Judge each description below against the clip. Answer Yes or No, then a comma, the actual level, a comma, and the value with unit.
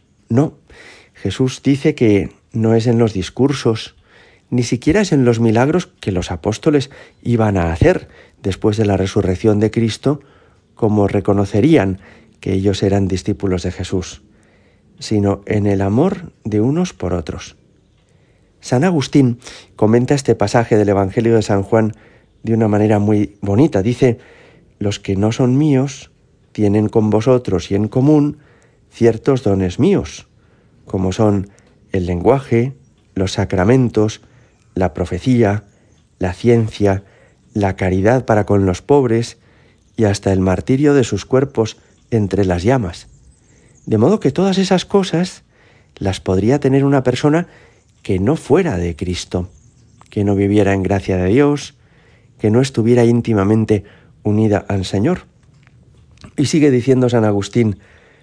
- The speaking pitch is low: Yes, low, 110 Hz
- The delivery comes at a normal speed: Yes, average, 140 wpm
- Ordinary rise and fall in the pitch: Yes, average, 4.1 semitones